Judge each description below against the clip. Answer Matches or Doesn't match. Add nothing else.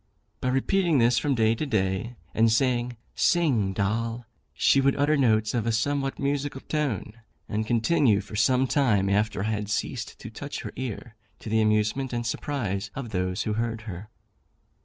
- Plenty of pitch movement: Doesn't match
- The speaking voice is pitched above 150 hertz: Doesn't match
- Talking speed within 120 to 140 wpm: Doesn't match